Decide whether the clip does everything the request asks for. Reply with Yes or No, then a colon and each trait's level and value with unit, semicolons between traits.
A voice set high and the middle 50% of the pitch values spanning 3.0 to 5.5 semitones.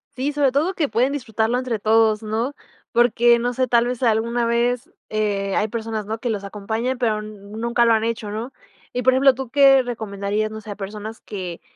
No: high, 230 Hz; narrow, 2.6 semitones